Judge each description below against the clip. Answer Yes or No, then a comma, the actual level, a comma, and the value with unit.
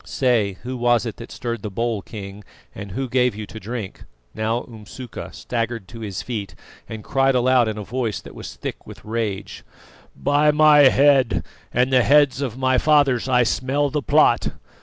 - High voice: No, low, 120 Hz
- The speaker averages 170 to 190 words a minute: Yes, average, 180 wpm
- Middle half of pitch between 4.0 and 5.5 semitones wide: No, average, 3.3 semitones